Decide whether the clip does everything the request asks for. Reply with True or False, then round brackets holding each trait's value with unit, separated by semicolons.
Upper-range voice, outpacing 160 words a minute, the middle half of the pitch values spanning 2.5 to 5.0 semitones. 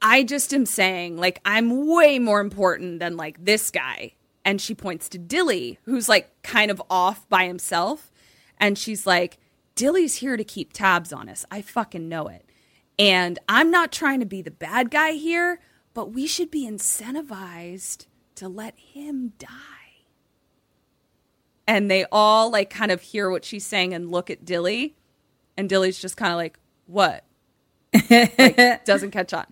False (205 Hz; 170 wpm; 5.4 semitones)